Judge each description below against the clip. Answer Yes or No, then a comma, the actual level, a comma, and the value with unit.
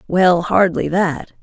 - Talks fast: No, slow, 125 wpm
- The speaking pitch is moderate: Yes, medium, 175 Hz